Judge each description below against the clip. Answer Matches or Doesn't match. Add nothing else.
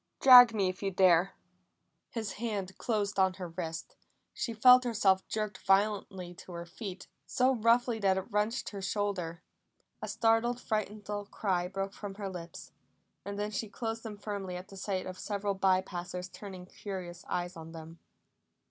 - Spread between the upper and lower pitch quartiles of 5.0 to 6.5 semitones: Doesn't match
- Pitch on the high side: Matches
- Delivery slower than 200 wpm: Matches